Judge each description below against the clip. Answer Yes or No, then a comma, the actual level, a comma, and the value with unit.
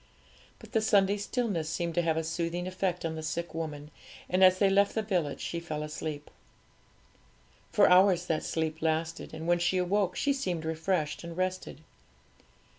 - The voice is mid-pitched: Yes, medium, 170 Hz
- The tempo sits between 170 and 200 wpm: Yes, average, 175 wpm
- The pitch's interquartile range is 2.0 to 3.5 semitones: Yes, average, 2.7 semitones